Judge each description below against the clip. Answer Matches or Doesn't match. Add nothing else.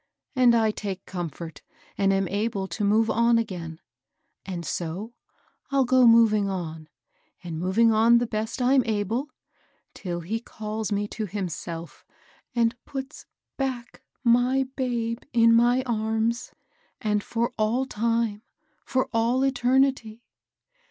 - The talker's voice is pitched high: Matches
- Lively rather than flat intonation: Doesn't match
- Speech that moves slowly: Matches